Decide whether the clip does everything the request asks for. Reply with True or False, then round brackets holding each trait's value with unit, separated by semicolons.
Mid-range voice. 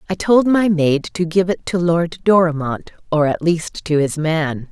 True (170 Hz)